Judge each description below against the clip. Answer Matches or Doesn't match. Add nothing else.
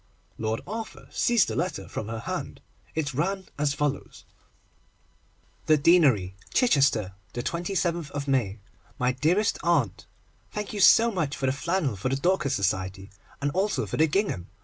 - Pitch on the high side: Doesn't match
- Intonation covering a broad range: Matches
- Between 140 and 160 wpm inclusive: Matches